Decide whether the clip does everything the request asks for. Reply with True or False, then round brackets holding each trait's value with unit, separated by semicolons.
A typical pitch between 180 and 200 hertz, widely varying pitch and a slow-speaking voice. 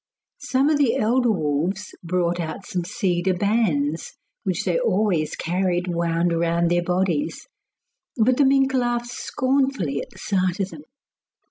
False (190 Hz; 6.0 semitones; 145 wpm)